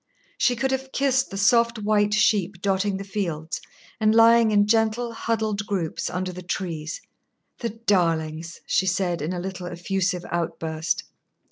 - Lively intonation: No, average, 4.0 semitones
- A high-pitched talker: Yes, high, 195 Hz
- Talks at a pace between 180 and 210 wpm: No, average, 150 wpm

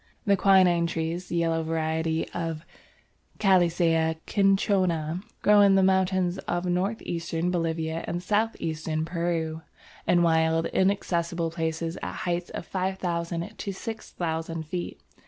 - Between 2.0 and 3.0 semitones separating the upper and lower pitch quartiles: Yes, narrow, 2.4 semitones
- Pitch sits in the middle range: Yes, medium, 170 Hz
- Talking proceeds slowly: Yes, slow, 125 wpm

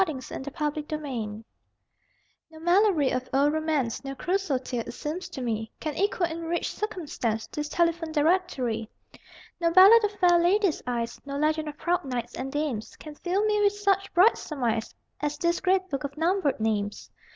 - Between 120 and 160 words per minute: No, average, 175 wpm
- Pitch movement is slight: No, average, 5.2 semitones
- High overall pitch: Yes, very high, 310 Hz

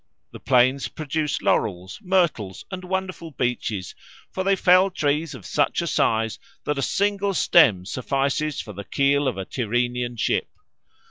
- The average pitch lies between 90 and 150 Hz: Yes, medium, 140 Hz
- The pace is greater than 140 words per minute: Yes, average, 150 wpm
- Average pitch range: No, wide, 6.7 semitones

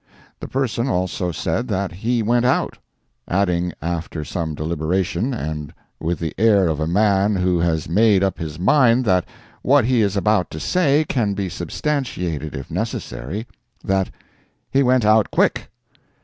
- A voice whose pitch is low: Yes, very low, 95 Hz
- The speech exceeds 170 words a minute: No, average, 150 wpm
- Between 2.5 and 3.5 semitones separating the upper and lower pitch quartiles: No, average, 5.2 semitones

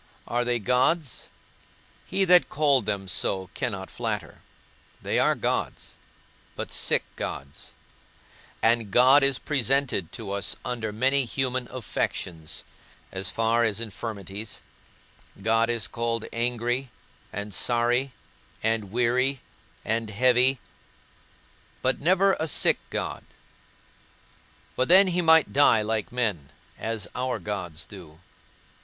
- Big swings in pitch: No, average, 3.9 semitones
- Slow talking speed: Yes, slow, 115 wpm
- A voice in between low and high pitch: No, low, 120 Hz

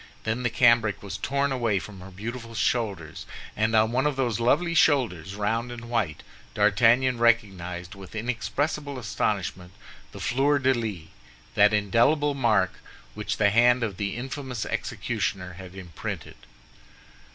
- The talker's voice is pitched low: Yes, low, 115 Hz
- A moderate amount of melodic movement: Yes, average, 4.2 semitones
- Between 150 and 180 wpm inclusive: No, slow, 135 wpm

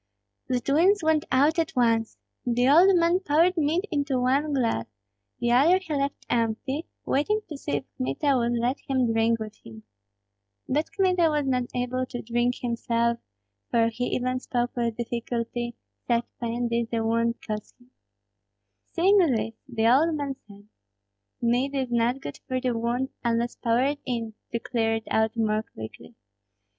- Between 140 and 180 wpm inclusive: Yes, average, 165 wpm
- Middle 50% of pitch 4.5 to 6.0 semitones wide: No, average, 3.5 semitones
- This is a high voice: Yes, high, 245 Hz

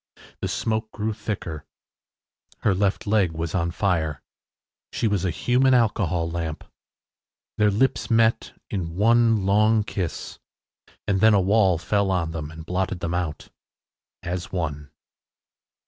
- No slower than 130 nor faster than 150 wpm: Yes, slow, 135 wpm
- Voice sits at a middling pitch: No, very low, 95 Hz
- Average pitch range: Yes, average, 4.3 semitones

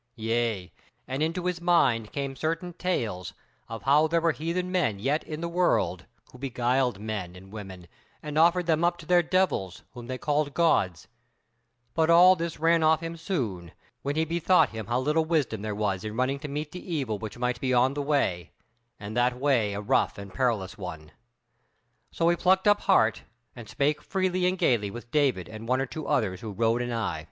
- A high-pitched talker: No, low, 135 Hz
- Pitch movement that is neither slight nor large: No, wide, 7.1 semitones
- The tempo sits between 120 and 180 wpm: No, average, 200 wpm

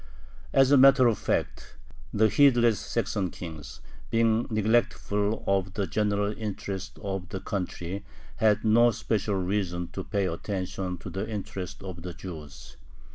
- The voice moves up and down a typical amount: Yes, average, 3.1 semitones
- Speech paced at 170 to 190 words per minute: No, average, 140 wpm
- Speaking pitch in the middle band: No, low, 100 Hz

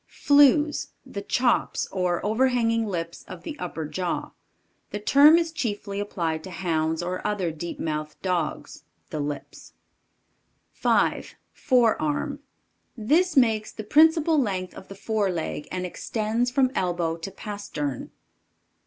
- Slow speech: Yes, slow, 130 wpm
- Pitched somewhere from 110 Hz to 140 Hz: No, high, 205 Hz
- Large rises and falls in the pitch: Yes, wide, 6.4 semitones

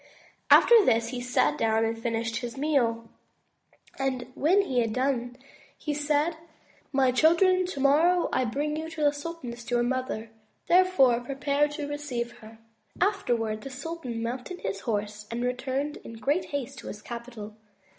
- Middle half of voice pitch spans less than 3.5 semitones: No, average, 4.3 semitones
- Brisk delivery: No, average, 165 wpm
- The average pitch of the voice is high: Yes, very high, 260 Hz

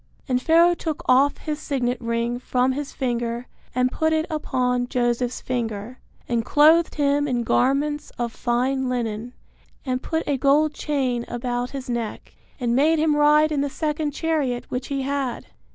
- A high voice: Yes, very high, 260 Hz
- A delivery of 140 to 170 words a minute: Yes, average, 165 wpm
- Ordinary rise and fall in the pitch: Yes, average, 3.4 semitones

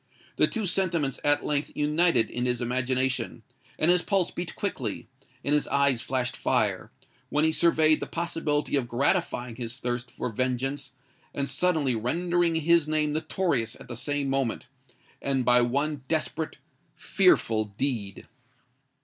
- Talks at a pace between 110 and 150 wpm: Yes, average, 140 wpm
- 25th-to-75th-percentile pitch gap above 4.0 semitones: Yes, average, 4.4 semitones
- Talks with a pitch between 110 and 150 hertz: Yes, medium, 140 Hz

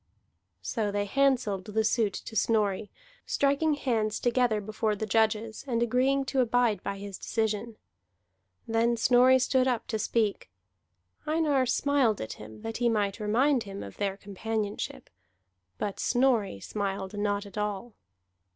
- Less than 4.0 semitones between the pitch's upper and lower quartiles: Yes, average, 3.4 semitones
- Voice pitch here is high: Yes, high, 220 Hz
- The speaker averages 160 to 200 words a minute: No, average, 140 wpm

